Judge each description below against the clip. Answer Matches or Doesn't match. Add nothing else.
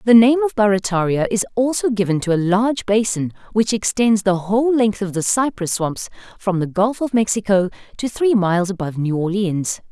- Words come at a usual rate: Matches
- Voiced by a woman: Matches